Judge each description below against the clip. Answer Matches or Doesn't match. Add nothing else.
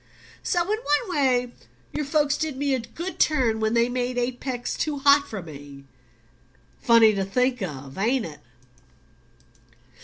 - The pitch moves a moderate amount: Matches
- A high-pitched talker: Matches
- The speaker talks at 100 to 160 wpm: Matches